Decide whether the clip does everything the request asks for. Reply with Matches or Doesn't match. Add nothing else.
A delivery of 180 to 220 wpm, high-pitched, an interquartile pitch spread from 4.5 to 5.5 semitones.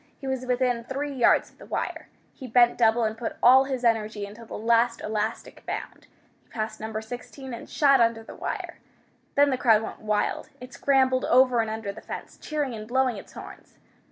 Doesn't match